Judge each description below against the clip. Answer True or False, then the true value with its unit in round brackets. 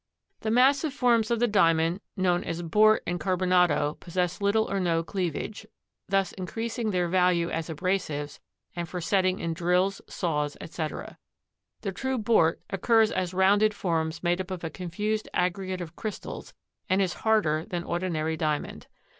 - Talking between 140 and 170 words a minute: True (155 wpm)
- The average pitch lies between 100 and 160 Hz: False (185 Hz)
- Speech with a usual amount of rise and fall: True (3.5 semitones)